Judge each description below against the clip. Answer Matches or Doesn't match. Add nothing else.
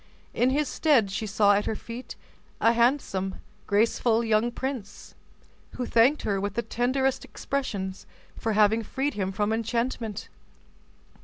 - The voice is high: Matches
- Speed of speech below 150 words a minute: Matches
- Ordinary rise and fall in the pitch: Matches